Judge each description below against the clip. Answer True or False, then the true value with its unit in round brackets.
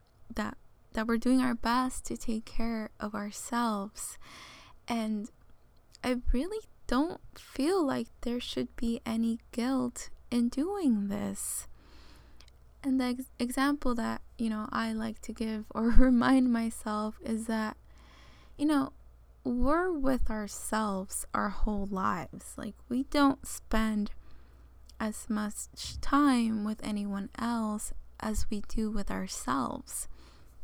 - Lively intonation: False (3.5 semitones)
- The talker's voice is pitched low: False (225 Hz)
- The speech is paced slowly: True (125 wpm)